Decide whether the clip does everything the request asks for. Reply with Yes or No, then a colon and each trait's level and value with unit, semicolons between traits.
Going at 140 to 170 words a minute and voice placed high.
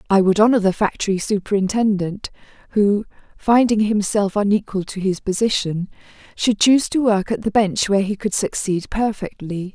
Yes: average, 155 wpm; high, 205 Hz